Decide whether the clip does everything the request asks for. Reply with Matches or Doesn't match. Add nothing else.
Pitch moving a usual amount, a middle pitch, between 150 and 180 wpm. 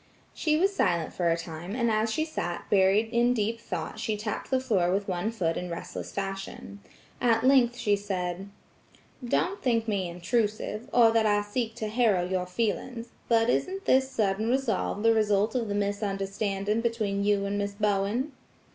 Doesn't match